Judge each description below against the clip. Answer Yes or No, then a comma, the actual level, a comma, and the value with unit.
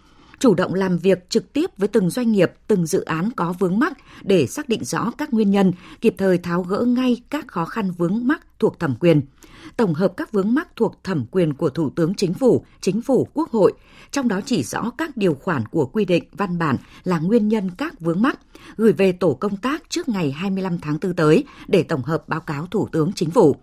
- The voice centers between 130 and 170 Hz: No, high, 195 Hz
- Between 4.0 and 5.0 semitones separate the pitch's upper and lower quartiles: No, wide, 5.5 semitones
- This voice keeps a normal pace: Yes, average, 230 wpm